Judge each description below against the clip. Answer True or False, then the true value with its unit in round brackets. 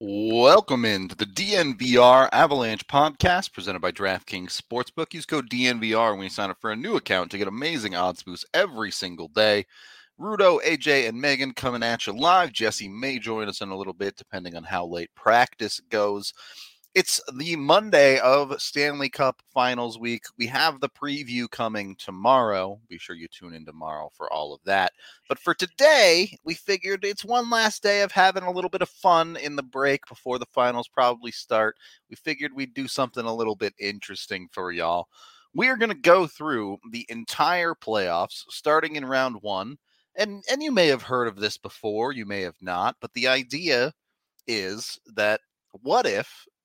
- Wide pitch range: True (6.9 semitones)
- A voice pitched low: True (125 Hz)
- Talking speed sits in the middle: True (185 wpm)